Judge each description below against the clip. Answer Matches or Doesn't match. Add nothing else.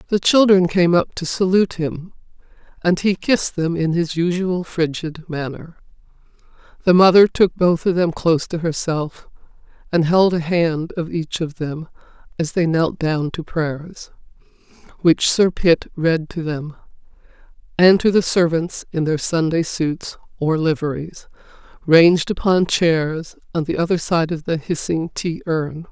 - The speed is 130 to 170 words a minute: Matches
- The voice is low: Doesn't match